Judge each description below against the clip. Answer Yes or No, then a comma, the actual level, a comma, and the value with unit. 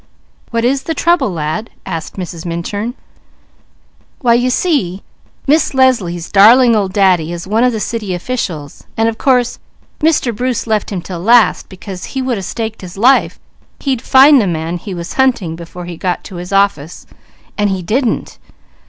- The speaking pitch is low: No, high, 210 Hz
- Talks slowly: No, average, 170 wpm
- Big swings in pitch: Yes, wide, 5.9 semitones